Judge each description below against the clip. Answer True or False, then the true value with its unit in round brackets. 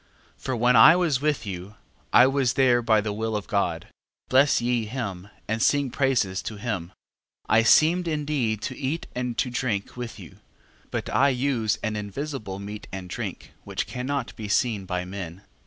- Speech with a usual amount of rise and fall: True (4.6 semitones)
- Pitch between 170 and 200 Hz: False (115 Hz)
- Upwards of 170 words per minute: True (185 wpm)